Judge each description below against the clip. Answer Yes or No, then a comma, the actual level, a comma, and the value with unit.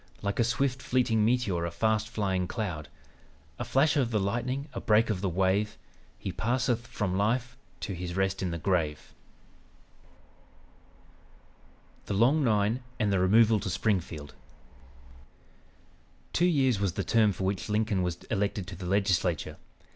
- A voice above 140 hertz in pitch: No, low, 105 Hz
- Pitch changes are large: No, average, 3.9 semitones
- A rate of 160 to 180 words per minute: No, average, 150 wpm